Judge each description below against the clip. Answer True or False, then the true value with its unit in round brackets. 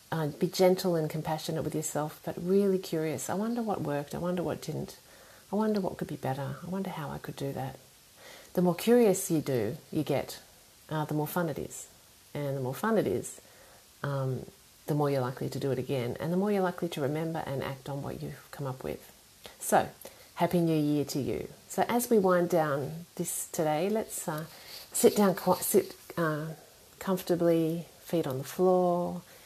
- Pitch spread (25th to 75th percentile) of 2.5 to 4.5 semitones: True (4.1 semitones)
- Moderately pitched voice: True (160 Hz)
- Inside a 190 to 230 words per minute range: True (200 wpm)